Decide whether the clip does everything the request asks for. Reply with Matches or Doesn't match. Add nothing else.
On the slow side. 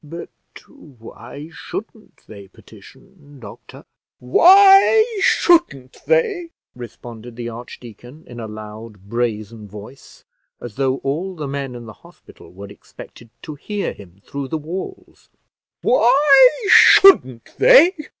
Matches